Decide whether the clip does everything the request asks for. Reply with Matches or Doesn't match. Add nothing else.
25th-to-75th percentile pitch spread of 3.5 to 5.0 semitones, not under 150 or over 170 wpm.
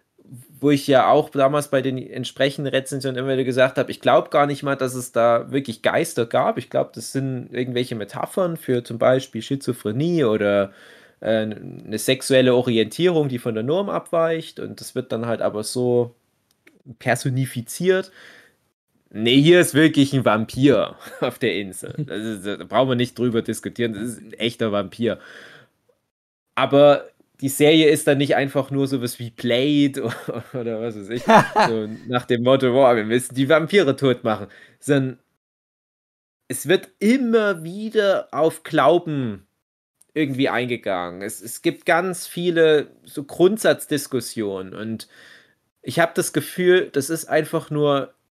Matches